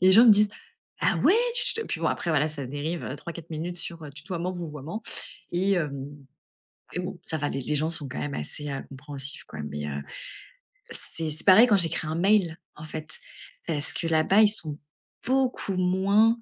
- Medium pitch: Yes, medium, 165 Hz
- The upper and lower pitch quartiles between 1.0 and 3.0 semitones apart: No, average, 4.3 semitones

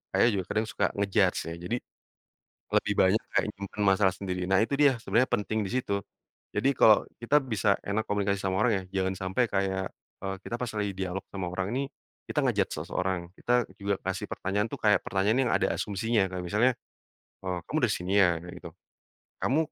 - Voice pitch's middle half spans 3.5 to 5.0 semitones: No, narrow, 2.6 semitones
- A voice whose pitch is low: Yes, low, 100 Hz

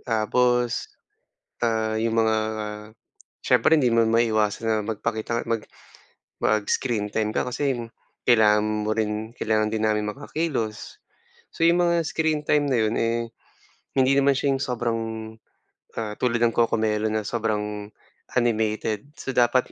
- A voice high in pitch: No, low, 115 Hz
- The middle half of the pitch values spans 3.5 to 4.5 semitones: No, narrow, 2.5 semitones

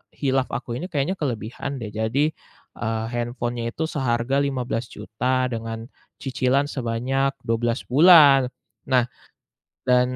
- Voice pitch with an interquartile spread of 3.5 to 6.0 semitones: No, average, 2.7 semitones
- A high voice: No, low, 125 Hz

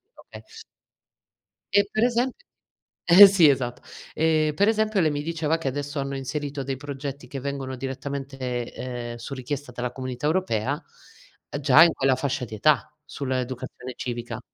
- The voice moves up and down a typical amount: Yes, average, 3.2 semitones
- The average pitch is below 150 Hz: Yes, medium, 140 Hz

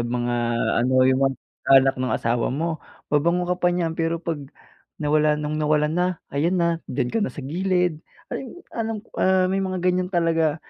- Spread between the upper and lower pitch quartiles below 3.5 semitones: No, average, 3.8 semitones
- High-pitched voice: No, medium, 165 Hz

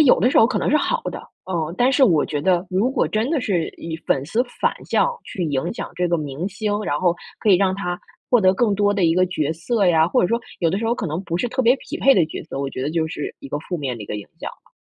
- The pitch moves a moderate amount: No, wide, 5.7 semitones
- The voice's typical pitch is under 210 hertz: Yes, medium, 185 Hz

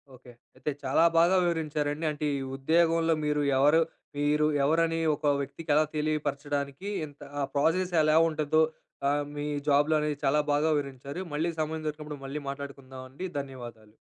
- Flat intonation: Yes, narrow, 2.1 semitones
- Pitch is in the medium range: Yes, medium, 150 Hz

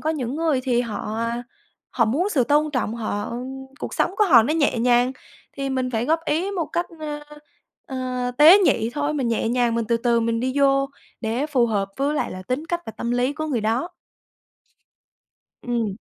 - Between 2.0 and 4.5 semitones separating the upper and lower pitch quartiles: Yes, average, 4.2 semitones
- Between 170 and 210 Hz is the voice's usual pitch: No, very high, 255 Hz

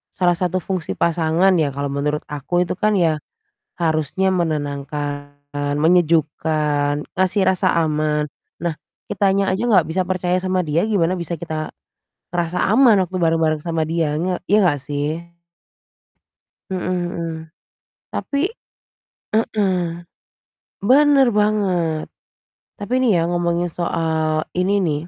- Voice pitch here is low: No, medium, 170 Hz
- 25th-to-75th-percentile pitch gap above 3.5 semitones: No, average, 3.1 semitones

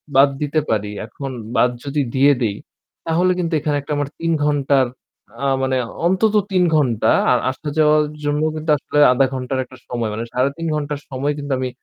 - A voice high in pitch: No, medium, 140 Hz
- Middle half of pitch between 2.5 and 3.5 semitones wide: Yes, average, 2.8 semitones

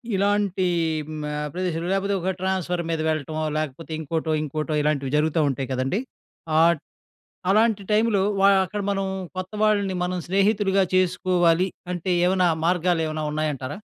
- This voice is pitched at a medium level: Yes, medium, 180 Hz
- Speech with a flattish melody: No, average, 3.8 semitones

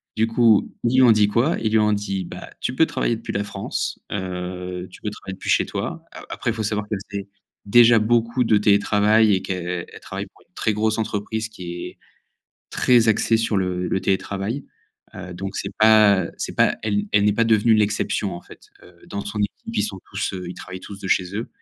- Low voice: Yes, low, 105 Hz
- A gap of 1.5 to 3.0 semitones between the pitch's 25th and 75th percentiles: Yes, narrow, 2.5 semitones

